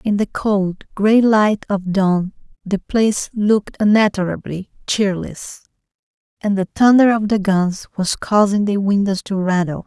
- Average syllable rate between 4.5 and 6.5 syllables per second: No, 4.3 syllables/s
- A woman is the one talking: Yes, female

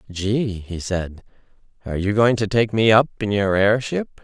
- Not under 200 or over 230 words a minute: No, average, 185 wpm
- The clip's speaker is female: No, male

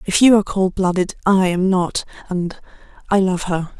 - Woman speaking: Yes, female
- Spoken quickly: No, average, 175 wpm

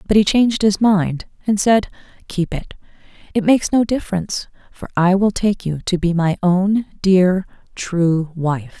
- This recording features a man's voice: No, female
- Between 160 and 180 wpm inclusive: Yes, average, 170 wpm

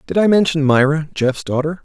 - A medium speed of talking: Yes, average, 195 wpm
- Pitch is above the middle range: No, medium, 155 Hz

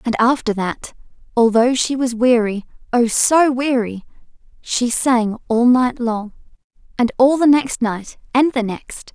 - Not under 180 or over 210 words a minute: No, average, 150 wpm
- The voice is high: Yes, high, 240 Hz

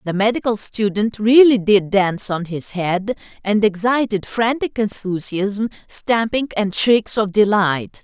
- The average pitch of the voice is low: No, high, 205 Hz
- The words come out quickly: No, slow, 135 wpm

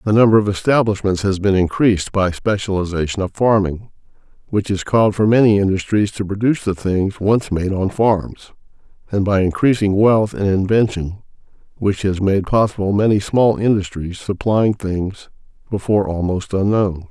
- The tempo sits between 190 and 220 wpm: No, average, 150 wpm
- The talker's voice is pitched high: No, low, 100 Hz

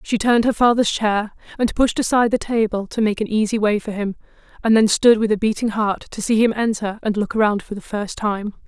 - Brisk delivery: Yes, fast, 240 wpm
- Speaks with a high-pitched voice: Yes, high, 215 Hz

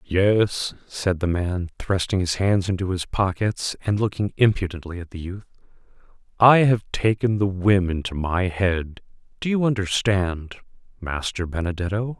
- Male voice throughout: Yes, male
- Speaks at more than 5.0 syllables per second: No, 4.4 syllables/s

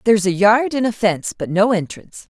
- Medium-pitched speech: No, high, 205 Hz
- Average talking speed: No, fast, 225 wpm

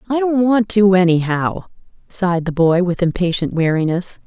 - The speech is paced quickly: No, average, 155 wpm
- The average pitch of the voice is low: No, medium, 185 Hz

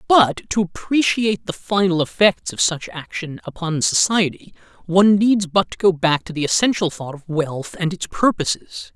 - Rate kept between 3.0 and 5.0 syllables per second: Yes, 4.8 syllables/s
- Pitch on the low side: No, medium, 180 Hz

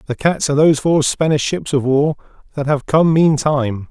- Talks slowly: No, average, 200 wpm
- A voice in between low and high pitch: Yes, medium, 145 Hz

